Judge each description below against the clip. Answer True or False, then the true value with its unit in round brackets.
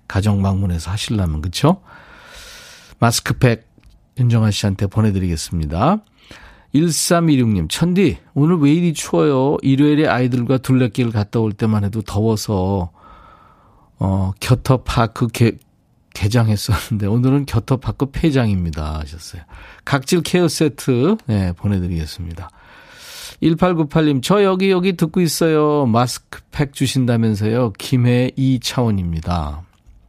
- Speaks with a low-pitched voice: True (120 Hz)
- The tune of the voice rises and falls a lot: True (6.9 semitones)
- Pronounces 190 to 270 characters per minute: True (265 characters per minute)